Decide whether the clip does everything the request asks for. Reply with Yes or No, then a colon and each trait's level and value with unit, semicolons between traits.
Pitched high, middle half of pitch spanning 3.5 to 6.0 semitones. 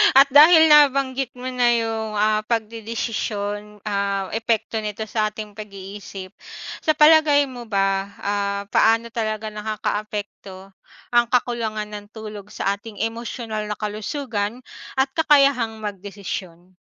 No: high, 215 Hz; average, 2.7 semitones